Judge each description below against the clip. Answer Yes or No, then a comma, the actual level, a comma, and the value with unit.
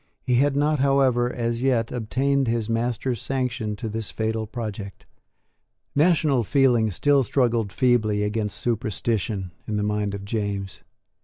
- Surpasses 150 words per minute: No, average, 140 wpm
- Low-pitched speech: Yes, low, 115 Hz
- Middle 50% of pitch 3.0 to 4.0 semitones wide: Yes, average, 3.6 semitones